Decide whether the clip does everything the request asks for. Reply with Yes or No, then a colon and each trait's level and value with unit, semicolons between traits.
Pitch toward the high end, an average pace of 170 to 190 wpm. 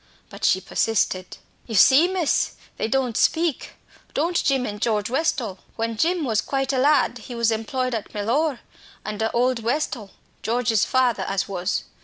No: high, 240 Hz; average, 160 wpm